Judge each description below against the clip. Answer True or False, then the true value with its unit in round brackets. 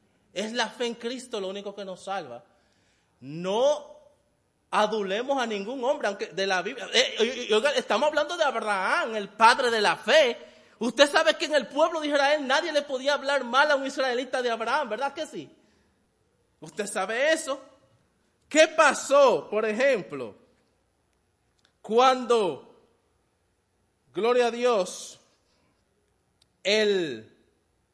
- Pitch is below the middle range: False (250 Hz)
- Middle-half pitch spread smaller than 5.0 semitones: False (5.3 semitones)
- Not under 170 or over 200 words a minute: False (135 wpm)